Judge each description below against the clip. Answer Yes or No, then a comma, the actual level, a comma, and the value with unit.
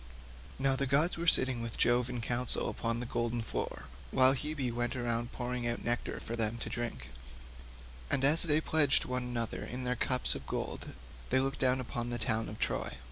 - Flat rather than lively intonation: Yes, narrow, 2.0 semitones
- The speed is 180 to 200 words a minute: Yes, average, 195 wpm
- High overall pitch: No, low, 125 Hz